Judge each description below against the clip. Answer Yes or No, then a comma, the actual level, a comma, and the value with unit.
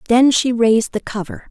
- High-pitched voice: Yes, high, 235 Hz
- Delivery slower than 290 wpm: Yes, average, 200 wpm